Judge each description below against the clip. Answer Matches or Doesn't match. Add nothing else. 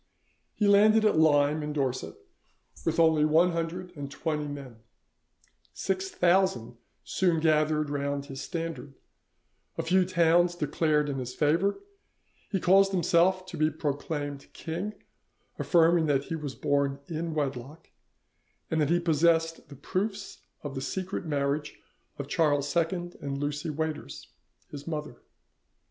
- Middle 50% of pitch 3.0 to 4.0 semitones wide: Matches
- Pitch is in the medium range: Matches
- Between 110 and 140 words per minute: Matches